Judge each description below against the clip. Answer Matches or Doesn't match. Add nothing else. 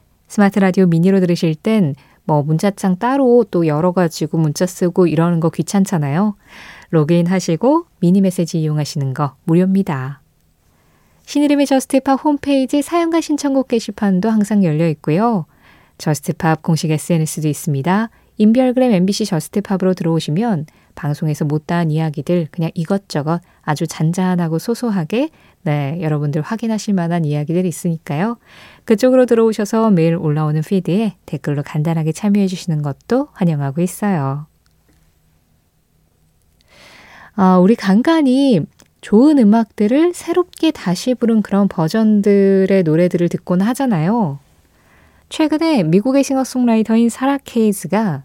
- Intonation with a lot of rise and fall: Matches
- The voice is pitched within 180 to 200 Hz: Matches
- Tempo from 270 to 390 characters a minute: Matches